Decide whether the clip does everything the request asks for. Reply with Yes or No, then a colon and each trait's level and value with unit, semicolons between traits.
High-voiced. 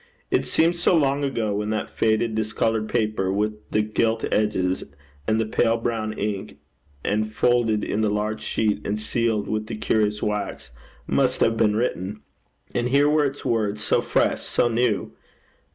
No: low, 110 Hz